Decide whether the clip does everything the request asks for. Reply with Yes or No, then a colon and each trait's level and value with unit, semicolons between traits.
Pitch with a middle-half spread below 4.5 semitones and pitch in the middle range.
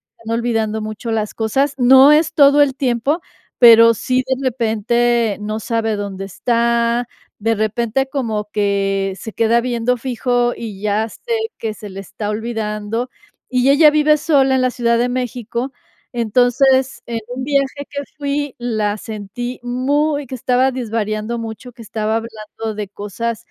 No: average, 3.0 semitones; high, 235 Hz